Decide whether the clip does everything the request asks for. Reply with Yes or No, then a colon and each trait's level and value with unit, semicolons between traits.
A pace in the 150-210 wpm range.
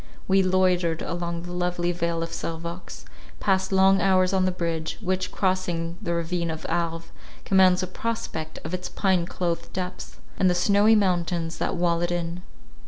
Yes: average, 170 wpm